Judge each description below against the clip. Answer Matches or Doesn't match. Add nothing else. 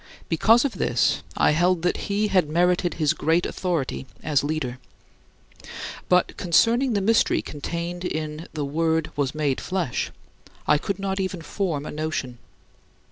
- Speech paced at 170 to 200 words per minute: Doesn't match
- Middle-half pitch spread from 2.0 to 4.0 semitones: Matches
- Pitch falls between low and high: Matches